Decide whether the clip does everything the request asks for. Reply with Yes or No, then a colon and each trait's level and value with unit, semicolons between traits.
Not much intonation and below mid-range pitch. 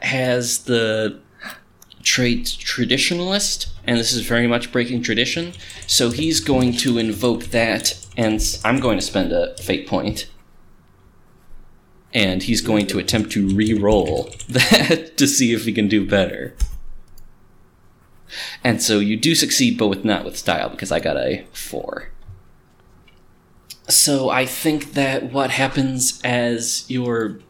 No: average, 3.4 semitones; low, 120 Hz